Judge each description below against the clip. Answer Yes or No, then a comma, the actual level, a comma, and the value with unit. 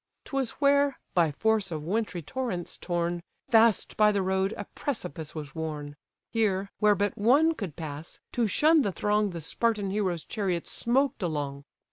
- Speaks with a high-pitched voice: Yes, high, 200 Hz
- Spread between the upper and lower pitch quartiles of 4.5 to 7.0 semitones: Yes, average, 5.2 semitones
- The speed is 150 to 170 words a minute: Yes, average, 160 wpm